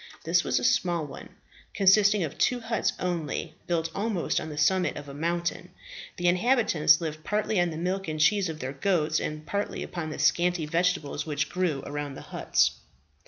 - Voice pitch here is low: No, medium, 170 Hz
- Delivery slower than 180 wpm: No, average, 185 wpm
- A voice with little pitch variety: No, average, 3.6 semitones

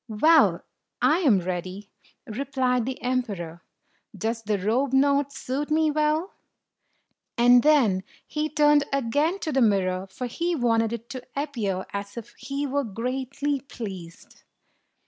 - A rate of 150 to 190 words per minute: No, slow, 135 wpm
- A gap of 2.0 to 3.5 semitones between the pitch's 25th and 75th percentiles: No, average, 5.3 semitones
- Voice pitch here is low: No, very high, 250 Hz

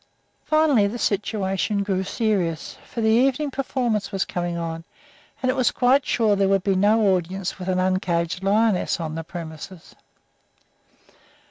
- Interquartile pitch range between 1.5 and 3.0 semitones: No, average, 3.9 semitones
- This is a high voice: Yes, high, 195 Hz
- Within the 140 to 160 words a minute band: Yes, average, 150 wpm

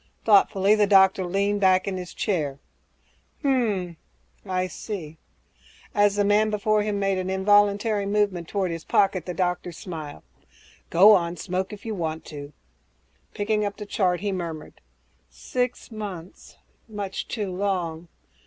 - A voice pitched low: No, high, 195 Hz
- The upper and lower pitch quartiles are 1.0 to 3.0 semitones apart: Yes, narrow, 2.6 semitones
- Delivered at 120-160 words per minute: Yes, average, 150 wpm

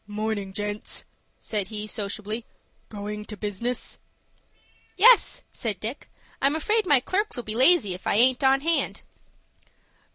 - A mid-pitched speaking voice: No, high, 220 Hz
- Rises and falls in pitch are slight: No, average, 4.9 semitones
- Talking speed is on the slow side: Yes, slow, 130 wpm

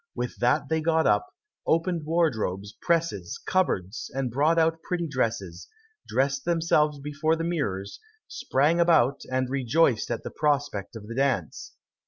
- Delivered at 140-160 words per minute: Yes, average, 145 wpm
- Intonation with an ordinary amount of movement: No, wide, 6.0 semitones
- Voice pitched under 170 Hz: Yes, medium, 140 Hz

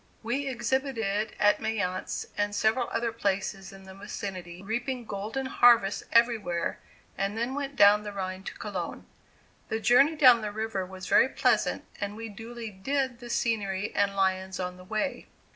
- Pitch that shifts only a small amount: No, average, 3.6 semitones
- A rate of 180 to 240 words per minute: No, average, 160 wpm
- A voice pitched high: Yes, high, 215 Hz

